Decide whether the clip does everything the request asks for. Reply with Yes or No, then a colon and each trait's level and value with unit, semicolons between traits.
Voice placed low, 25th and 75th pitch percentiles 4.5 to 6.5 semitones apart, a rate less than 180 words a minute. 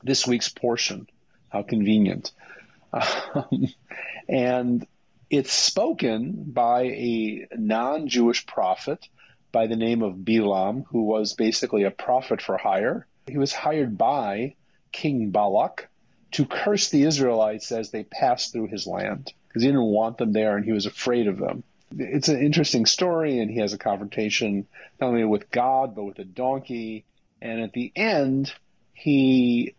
No: low, 120 Hz; average, 3.3 semitones; average, 155 wpm